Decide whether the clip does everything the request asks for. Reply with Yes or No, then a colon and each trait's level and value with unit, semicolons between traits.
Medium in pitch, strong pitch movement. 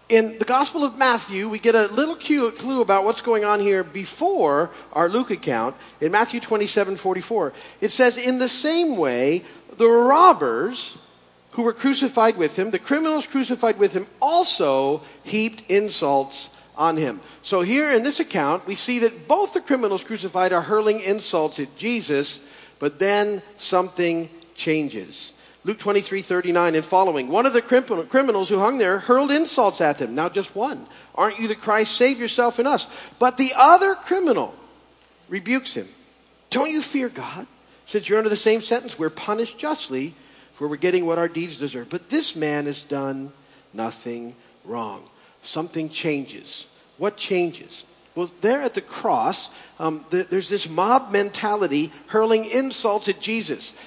No: high, 210 Hz; wide, 6.2 semitones